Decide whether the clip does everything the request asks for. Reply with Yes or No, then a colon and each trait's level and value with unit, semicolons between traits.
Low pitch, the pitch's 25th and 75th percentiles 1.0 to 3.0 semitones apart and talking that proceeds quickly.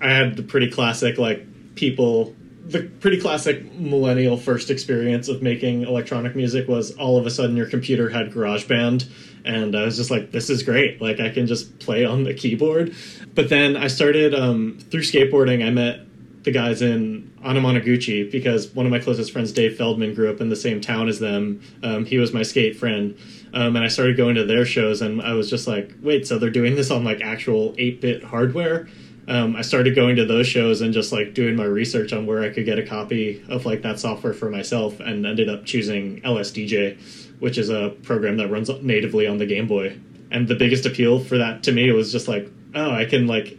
Yes: low, 120 Hz; narrow, 2.5 semitones; fast, 220 wpm